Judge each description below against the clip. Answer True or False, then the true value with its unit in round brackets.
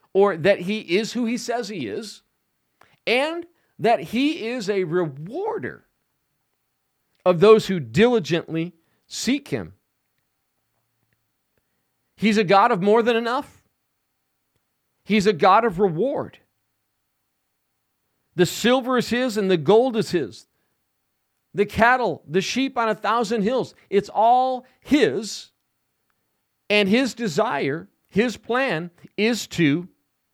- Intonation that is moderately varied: True (4.9 semitones)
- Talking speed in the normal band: False (120 wpm)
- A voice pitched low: False (210 Hz)